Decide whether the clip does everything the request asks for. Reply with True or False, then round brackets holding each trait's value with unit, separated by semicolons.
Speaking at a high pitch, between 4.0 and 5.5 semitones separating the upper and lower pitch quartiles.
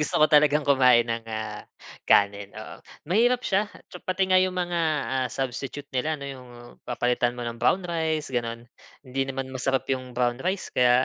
False (135 Hz; 4.5 semitones)